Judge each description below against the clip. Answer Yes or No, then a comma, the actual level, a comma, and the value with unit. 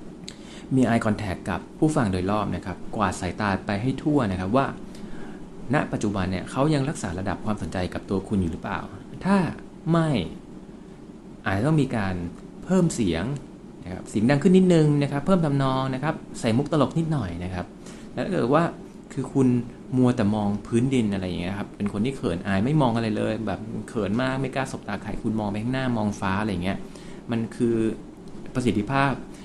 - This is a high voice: No, low, 115 Hz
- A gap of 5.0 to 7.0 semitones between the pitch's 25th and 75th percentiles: Yes, wide, 5.5 semitones